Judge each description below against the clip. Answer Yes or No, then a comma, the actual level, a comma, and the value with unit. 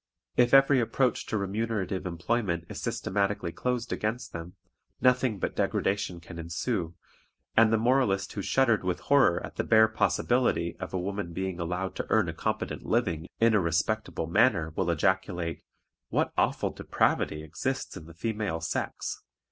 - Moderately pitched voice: No, low, 100 Hz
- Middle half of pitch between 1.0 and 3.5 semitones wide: No, average, 5.0 semitones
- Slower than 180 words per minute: Yes, average, 155 wpm